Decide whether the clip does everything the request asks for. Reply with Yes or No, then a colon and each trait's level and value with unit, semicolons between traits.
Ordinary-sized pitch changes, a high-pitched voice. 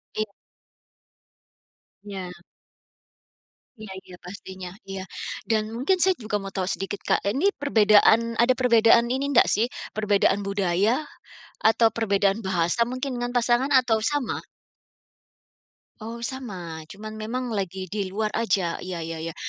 Yes: average, 3.6 semitones; high, 215 Hz